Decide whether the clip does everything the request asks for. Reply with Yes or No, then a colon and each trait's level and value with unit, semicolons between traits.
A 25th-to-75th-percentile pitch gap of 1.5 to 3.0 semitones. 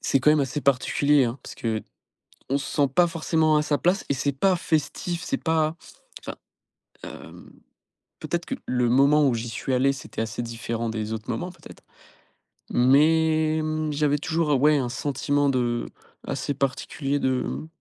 No: average, 3.6 semitones